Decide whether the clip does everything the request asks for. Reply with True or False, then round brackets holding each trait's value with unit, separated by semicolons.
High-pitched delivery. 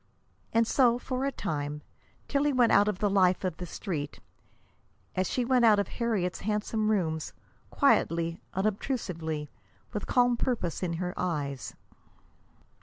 True (195 Hz)